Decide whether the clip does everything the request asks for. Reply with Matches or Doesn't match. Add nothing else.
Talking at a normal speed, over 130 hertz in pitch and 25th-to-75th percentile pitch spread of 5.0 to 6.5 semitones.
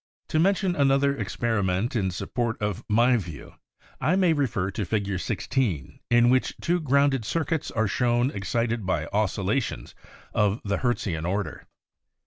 Doesn't match